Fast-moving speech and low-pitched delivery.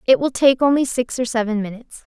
No: fast, 220 wpm; high, 240 Hz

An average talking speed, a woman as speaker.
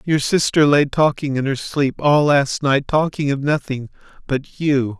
No: average, 180 wpm; male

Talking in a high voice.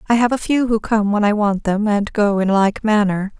Yes: high, 210 Hz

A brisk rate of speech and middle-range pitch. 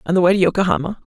Yes: fast, 270 wpm; medium, 170 Hz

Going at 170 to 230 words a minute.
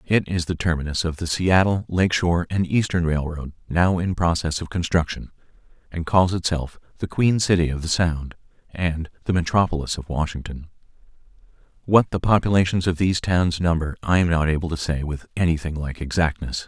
Yes: average, 175 wpm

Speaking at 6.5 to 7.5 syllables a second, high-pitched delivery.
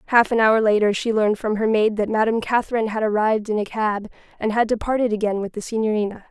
Yes: 6.8 syllables/s; high, 215 Hz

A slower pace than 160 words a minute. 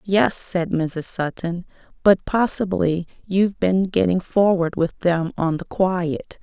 Yes: average, 140 wpm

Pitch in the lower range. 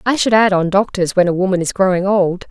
No: high, 190 Hz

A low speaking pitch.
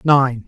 Yes: low, 130 Hz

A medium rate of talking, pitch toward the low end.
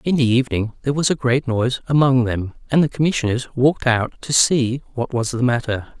No: fast, 210 wpm; low, 125 Hz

